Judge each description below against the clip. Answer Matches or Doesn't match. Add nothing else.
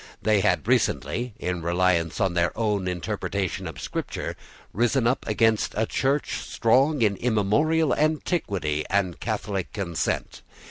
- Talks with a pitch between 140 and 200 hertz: Doesn't match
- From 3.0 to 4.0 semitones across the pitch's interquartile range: Doesn't match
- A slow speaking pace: Matches